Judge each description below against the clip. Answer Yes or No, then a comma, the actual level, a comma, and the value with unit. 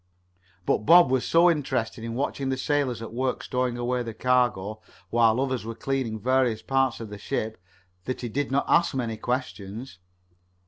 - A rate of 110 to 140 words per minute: No, average, 175 wpm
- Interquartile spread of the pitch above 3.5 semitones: No, average, 2.9 semitones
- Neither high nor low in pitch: No, low, 125 Hz